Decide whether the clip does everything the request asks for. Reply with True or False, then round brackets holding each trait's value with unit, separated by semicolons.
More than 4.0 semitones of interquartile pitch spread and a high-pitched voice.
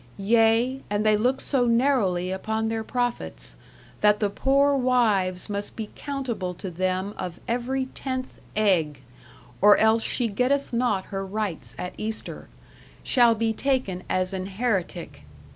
True (4.5 semitones; 220 Hz)